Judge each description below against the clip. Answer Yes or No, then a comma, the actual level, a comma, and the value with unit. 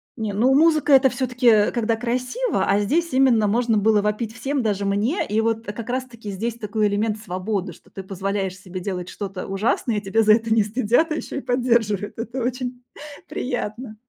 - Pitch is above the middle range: Yes, high, 225 Hz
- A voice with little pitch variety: No, average, 3.3 semitones